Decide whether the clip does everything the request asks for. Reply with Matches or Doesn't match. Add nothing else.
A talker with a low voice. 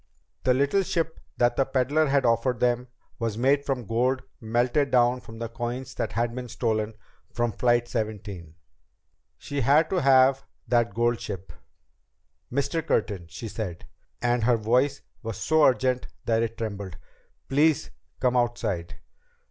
Matches